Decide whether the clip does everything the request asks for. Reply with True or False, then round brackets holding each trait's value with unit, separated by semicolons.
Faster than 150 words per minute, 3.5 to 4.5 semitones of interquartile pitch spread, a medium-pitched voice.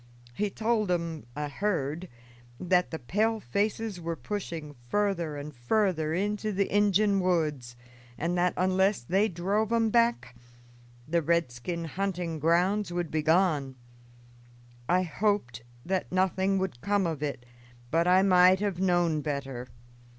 False (135 wpm; 4.2 semitones; 180 Hz)